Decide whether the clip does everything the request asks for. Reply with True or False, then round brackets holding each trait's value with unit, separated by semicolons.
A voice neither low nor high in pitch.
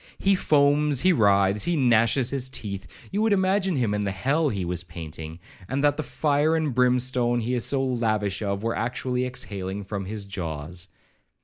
False (120 Hz)